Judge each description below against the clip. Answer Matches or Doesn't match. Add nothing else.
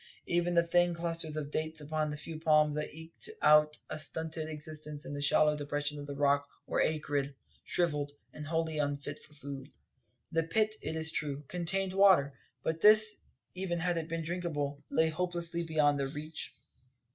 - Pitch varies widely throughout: Doesn't match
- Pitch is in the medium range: Matches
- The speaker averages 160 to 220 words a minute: Matches